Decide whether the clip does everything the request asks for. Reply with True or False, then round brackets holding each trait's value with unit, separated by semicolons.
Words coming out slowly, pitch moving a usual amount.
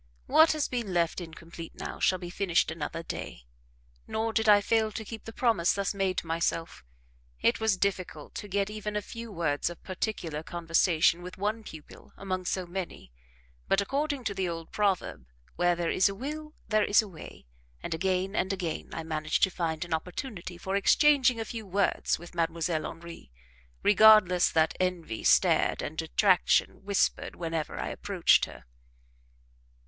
False (170 wpm; 4.0 semitones)